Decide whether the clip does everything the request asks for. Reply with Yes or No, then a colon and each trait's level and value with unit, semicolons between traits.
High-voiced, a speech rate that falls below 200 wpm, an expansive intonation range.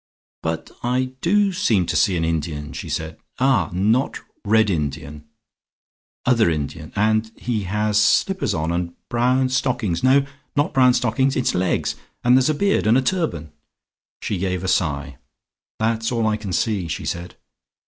No: low, 105 Hz; average, 165 wpm; wide, 6.9 semitones